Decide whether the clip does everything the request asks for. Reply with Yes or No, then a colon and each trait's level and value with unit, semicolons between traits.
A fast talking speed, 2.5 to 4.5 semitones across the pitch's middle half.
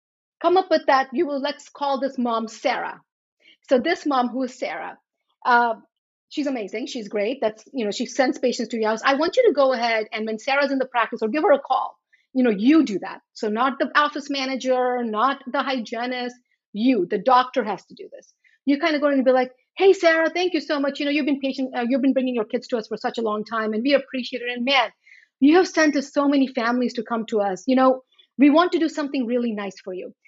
Yes: fast, 250 wpm; average, 3.4 semitones